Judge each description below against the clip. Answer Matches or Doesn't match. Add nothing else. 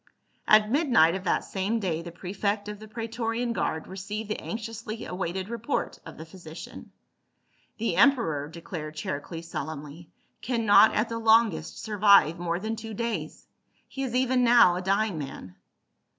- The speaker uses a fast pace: Doesn't match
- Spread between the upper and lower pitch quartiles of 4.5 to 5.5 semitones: Matches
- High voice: Matches